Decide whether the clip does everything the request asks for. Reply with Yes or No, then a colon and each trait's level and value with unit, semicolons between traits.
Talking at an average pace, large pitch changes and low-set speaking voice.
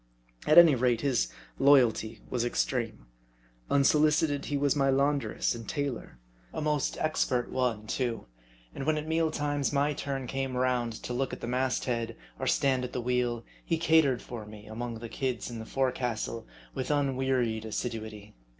No: average, 170 wpm; average, 3.3 semitones; low, 130 Hz